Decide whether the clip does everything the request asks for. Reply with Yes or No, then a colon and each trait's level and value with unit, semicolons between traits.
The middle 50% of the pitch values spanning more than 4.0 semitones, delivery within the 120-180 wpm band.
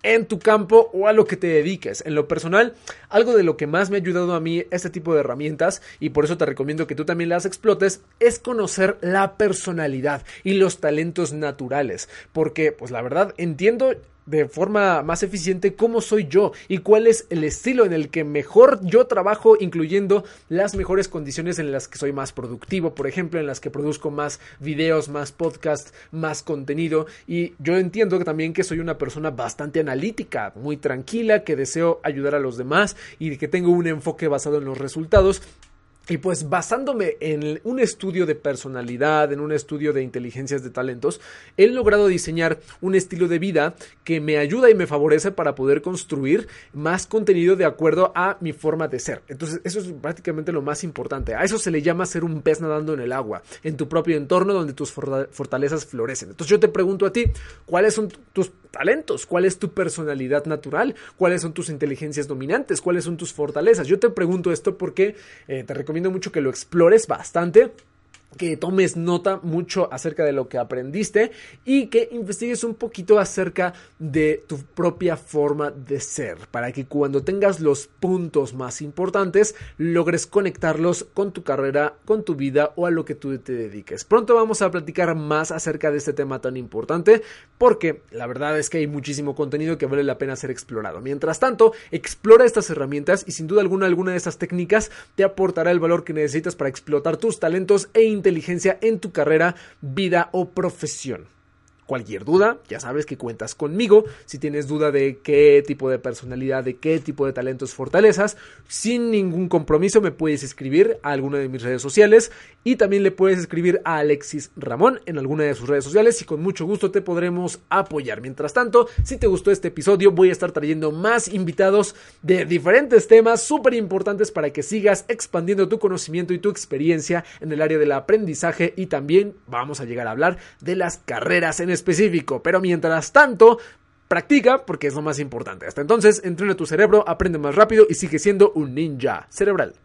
No: average, 4.8 semitones; fast, 190 wpm